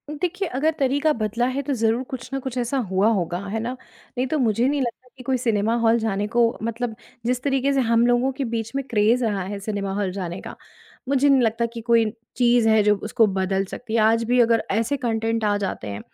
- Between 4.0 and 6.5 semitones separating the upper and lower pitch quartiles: No, average, 3.1 semitones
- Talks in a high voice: Yes, high, 230 Hz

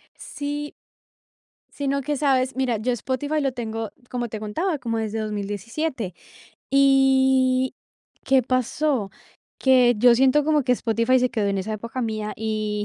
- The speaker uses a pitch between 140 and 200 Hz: No, very high, 250 Hz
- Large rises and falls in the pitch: No, average, 3.6 semitones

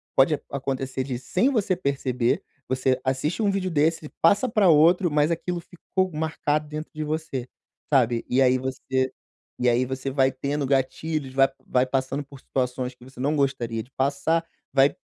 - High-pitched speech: No, medium, 140 Hz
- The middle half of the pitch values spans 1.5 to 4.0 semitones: Yes, average, 3.3 semitones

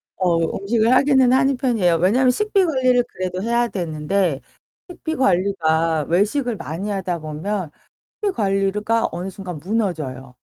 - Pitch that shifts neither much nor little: No, wide, 6.2 semitones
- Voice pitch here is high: Yes, high, 195 Hz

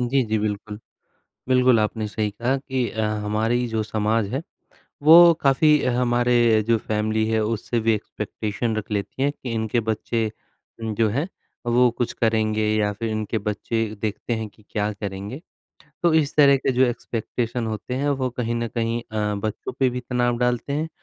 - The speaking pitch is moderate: No, low, 115 Hz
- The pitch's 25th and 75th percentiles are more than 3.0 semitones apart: No, narrow, 2.5 semitones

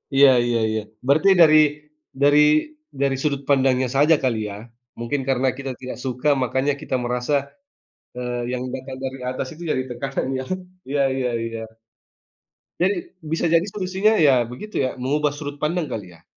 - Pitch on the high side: No, low, 135 Hz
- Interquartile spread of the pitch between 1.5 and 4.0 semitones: Yes, average, 3.3 semitones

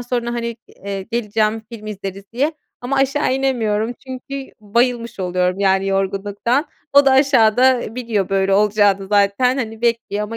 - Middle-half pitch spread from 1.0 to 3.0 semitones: No, average, 3.8 semitones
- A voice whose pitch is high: Yes, high, 225 Hz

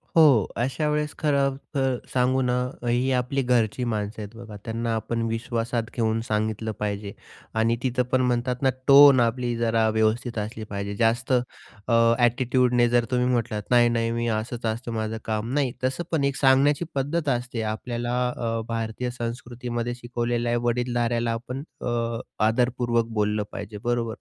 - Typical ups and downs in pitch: No, narrow, 1.8 semitones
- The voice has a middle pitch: No, low, 120 Hz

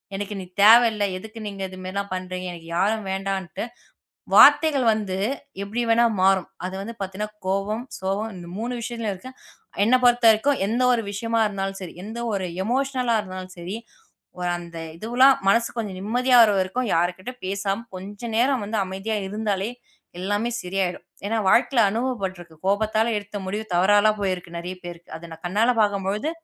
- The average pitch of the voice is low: No, high, 205 Hz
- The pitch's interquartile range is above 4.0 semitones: No, average, 3.3 semitones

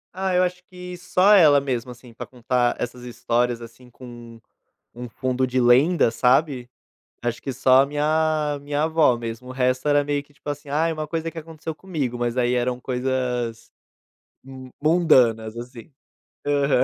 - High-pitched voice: No, low, 130 Hz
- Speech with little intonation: No, average, 3.9 semitones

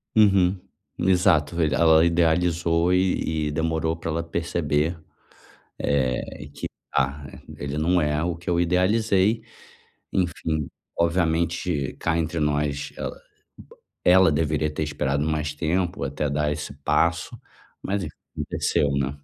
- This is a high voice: No, very low, 80 Hz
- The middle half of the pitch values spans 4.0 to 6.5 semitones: No, average, 2.9 semitones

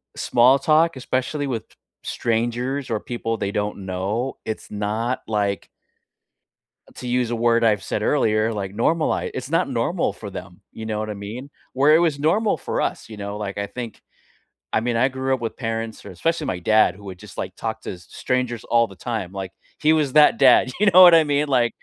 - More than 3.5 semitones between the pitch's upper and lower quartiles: Yes, average, 4.1 semitones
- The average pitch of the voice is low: Yes, low, 115 Hz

